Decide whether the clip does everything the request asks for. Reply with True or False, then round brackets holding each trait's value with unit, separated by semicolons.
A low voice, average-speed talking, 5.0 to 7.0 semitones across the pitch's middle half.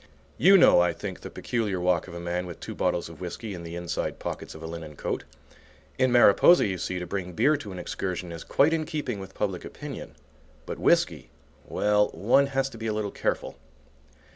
False (95 Hz; 210 wpm; 5.5 semitones)